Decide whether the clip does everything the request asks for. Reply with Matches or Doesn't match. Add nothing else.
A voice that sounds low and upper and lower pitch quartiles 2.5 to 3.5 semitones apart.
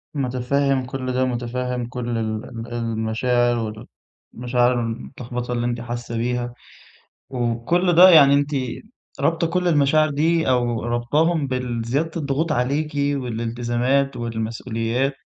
Matches